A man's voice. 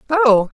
No: female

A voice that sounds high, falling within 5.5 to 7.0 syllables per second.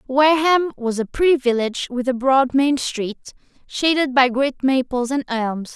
No: very high, 265 Hz; 4.6 syllables/s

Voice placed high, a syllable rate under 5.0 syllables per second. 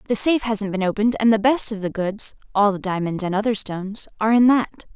No: high, 210 Hz; 6.1 syllables/s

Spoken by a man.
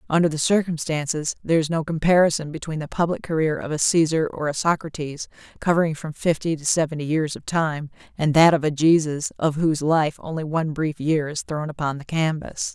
No: female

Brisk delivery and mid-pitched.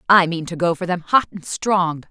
Yes: fast, 255 wpm; medium, 175 Hz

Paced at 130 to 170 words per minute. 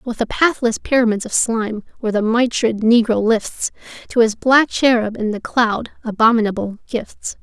Yes: average, 160 wpm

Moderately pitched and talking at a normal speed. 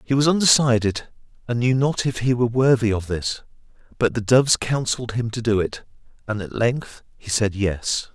No: low, 115 Hz; average, 190 wpm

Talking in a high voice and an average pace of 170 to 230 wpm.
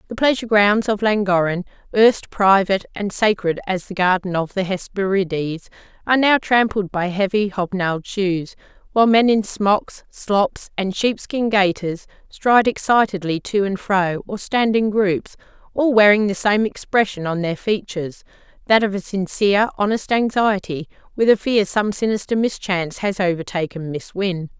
No: high, 200 Hz; average, 150 wpm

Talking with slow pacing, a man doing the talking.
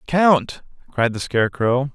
Yes: slow, 125 wpm; male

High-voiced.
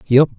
No: low, 125 Hz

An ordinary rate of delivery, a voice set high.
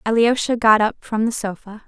Yes: average, 190 wpm; high, 220 Hz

